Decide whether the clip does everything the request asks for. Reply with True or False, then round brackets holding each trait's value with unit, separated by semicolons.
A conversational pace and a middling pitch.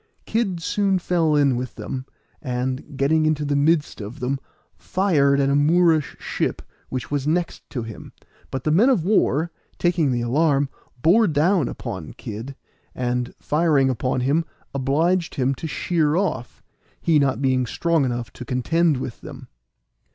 True (155 wpm; 145 Hz)